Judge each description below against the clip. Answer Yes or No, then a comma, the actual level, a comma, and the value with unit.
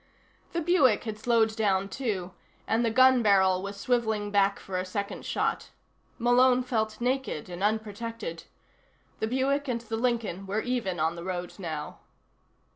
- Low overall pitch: No, high, 220 Hz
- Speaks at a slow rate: No, average, 155 wpm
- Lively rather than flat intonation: No, average, 4.1 semitones